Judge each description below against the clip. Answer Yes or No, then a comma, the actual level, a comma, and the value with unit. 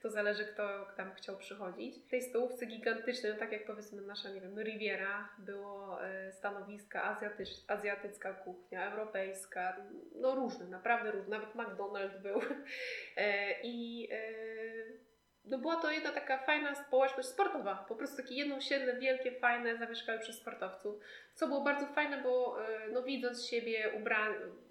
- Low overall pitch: No, high, 225 Hz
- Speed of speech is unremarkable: Yes, average, 150 wpm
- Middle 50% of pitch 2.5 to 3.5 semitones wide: No, average, 4.1 semitones